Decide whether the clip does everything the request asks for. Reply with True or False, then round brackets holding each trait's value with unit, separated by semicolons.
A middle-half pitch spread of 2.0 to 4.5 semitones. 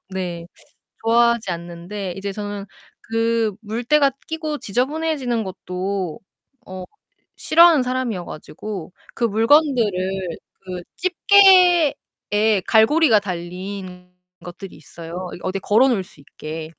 False (5.4 semitones)